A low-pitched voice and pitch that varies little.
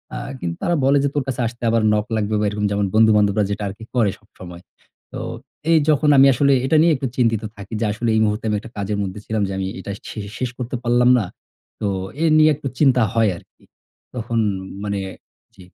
No: low, 110 Hz; average, 3.5 semitones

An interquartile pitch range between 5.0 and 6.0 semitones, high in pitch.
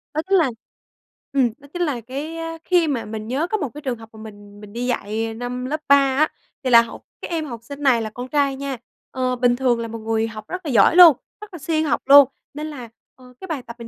No: average, 4.3 semitones; very high, 255 Hz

